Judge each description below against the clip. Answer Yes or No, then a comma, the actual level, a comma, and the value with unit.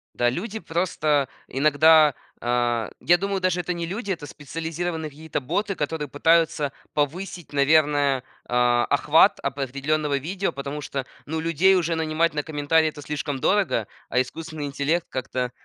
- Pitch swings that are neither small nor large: Yes, average, 3.2 semitones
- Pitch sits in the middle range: Yes, medium, 155 Hz